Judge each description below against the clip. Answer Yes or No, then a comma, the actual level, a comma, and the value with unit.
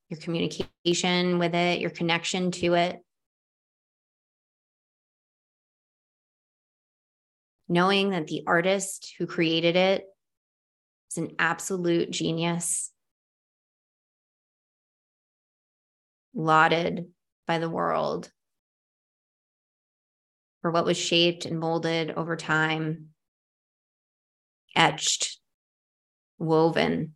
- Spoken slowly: Yes, slow, 75 wpm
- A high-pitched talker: No, medium, 170 Hz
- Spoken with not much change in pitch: Yes, narrow, 1.7 semitones